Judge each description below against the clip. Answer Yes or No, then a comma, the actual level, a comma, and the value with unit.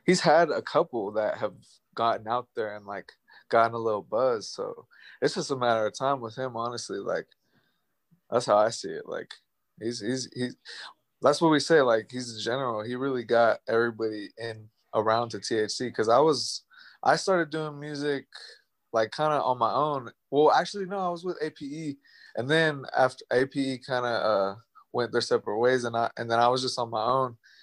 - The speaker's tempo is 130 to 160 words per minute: No, average, 200 wpm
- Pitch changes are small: No, average, 4.7 semitones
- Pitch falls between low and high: No, low, 125 Hz